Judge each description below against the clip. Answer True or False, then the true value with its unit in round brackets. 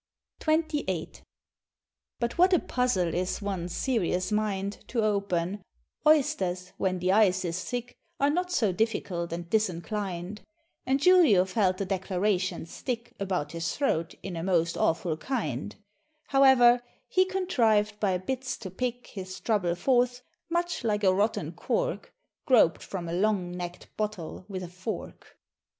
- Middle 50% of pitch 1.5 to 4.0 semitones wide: False (5.3 semitones)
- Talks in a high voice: True (200 Hz)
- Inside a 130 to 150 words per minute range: True (140 wpm)